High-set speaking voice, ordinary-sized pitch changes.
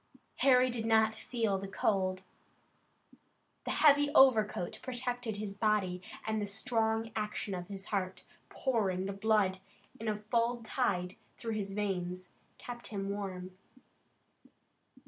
Yes: high, 215 Hz; average, 3.0 semitones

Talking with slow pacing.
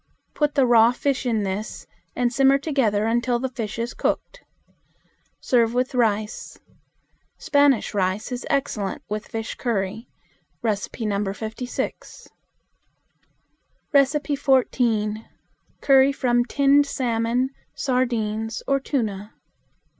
Yes: slow, 100 wpm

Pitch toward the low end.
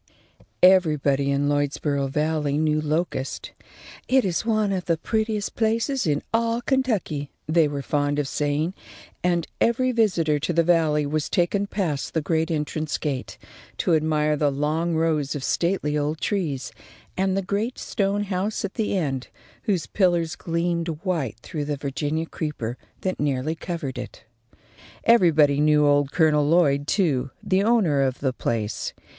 No: medium, 160 Hz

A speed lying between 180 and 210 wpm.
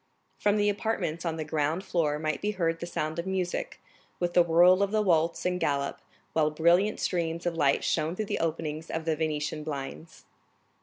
Yes: average, 195 wpm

